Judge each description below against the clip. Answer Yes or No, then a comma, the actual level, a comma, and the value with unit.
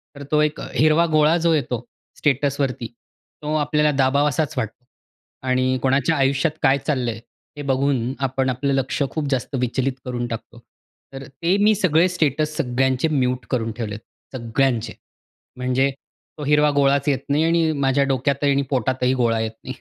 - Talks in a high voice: No, low, 135 Hz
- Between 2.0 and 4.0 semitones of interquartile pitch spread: Yes, average, 2.8 semitones